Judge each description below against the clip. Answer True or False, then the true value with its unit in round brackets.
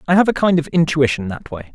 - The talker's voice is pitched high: False (150 Hz)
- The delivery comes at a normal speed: False (275 wpm)